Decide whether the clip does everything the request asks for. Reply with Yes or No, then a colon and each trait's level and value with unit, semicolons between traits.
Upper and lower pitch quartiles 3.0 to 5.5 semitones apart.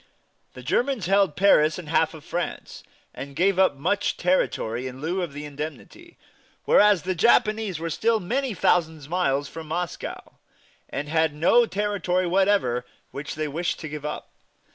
Yes: average, 4.8 semitones